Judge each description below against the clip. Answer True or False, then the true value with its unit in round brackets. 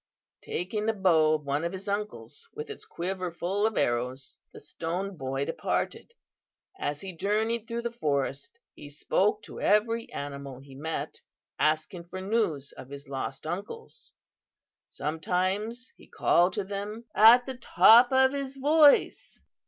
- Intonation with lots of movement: True (6.8 semitones)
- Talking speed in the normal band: True (150 wpm)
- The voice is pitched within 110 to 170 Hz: False (185 Hz)